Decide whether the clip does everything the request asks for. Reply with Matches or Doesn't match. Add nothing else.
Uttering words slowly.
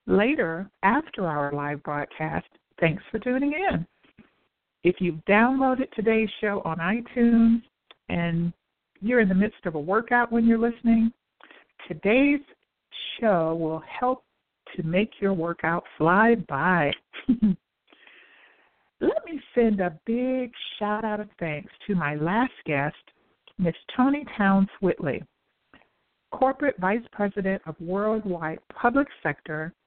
Matches